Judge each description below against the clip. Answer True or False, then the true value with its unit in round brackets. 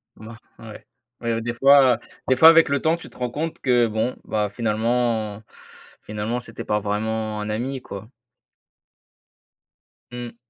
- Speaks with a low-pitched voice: True (115 Hz)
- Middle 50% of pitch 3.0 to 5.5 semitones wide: False (2.6 semitones)